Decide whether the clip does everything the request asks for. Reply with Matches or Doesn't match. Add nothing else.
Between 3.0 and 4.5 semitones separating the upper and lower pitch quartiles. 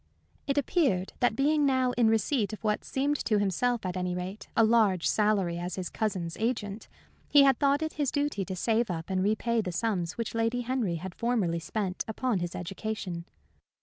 Doesn't match